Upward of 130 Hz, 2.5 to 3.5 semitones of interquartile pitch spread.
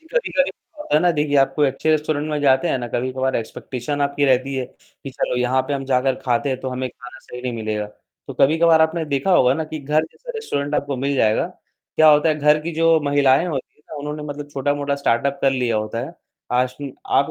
Yes: medium, 140 Hz; average, 2.8 semitones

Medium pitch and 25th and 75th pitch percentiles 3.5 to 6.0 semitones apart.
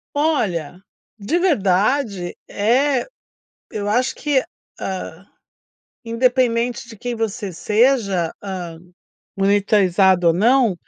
No: high, 210 Hz; average, 4.8 semitones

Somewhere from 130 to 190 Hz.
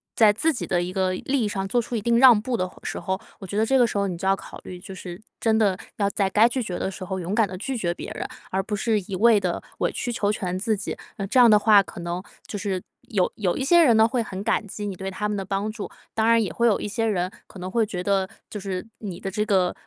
No: high, 205 Hz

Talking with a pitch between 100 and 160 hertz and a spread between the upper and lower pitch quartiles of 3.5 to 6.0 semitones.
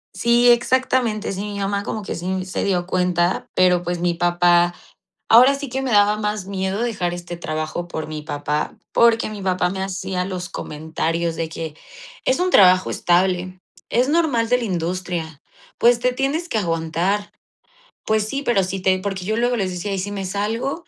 No: high, 190 Hz; average, 4.3 semitones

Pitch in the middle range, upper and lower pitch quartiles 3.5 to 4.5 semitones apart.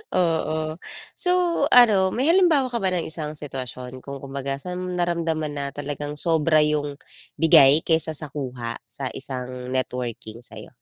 Yes: medium, 150 Hz; average, 3.9 semitones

